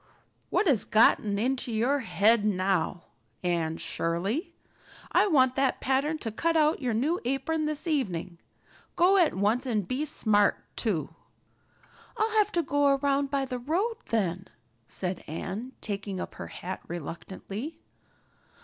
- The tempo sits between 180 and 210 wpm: No, average, 140 wpm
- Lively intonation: Yes, wide, 6.8 semitones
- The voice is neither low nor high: No, high, 245 Hz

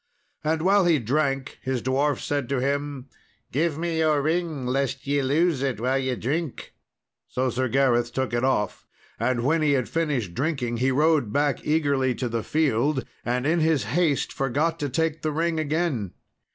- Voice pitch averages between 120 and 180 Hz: Yes, medium, 140 Hz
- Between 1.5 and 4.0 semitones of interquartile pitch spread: Yes, average, 3.6 semitones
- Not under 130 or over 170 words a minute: No, average, 180 wpm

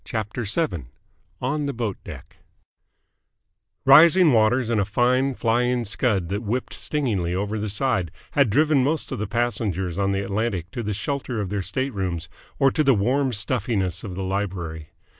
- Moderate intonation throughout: Yes, average, 4.9 semitones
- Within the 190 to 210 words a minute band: No, average, 165 wpm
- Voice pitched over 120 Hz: No, low, 110 Hz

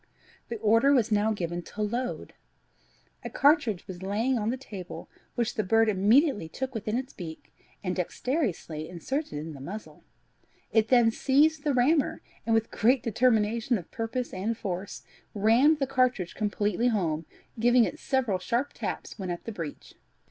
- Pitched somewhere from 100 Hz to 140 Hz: No, high, 225 Hz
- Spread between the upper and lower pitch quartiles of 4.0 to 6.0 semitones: Yes, average, 4.9 semitones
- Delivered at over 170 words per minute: No, average, 165 wpm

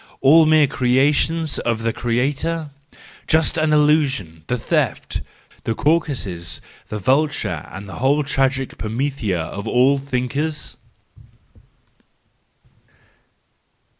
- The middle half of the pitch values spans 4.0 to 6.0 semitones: Yes, average, 4.7 semitones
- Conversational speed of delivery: No, slow, 105 wpm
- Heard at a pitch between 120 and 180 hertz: Yes, low, 135 Hz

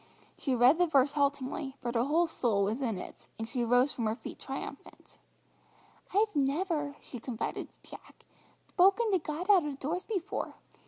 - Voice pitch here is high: Yes, very high, 280 Hz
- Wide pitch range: Yes, wide, 5.8 semitones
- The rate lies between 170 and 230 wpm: Yes, average, 175 wpm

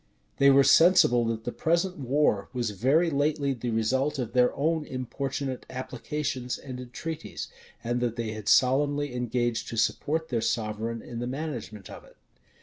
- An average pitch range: Yes, average, 3.7 semitones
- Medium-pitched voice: No, low, 130 Hz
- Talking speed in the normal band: Yes, average, 160 wpm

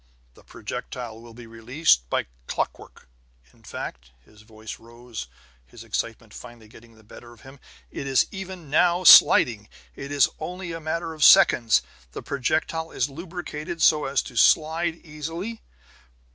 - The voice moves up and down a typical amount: No, wide, 6.1 semitones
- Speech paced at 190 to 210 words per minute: No, average, 150 wpm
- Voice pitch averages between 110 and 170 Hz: Yes, low, 135 Hz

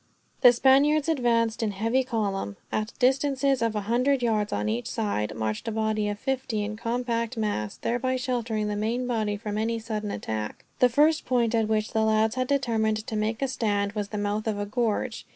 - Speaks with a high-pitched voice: Yes, high, 220 Hz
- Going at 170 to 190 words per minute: No, fast, 205 wpm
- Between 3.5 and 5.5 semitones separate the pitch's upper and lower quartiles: No, average, 2.9 semitones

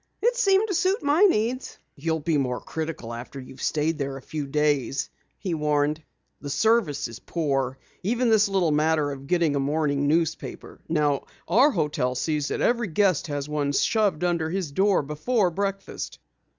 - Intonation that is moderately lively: No, wide, 5.7 semitones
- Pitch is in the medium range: Yes, medium, 155 Hz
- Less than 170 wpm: No, average, 175 wpm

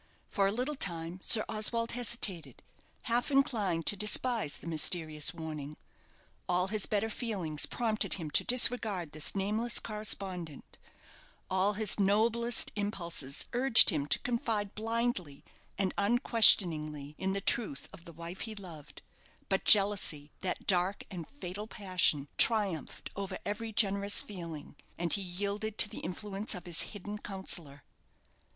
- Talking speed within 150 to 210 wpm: No, average, 140 wpm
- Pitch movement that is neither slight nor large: Yes, average, 4.4 semitones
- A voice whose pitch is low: No, high, 195 Hz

